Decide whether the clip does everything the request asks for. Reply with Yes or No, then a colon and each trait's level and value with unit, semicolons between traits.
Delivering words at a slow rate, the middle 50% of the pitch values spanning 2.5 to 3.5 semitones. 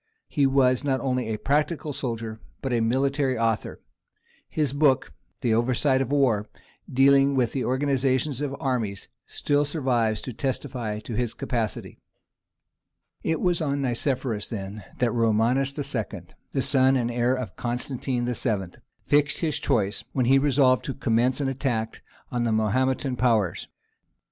No: average, 145 wpm; average, 3.0 semitones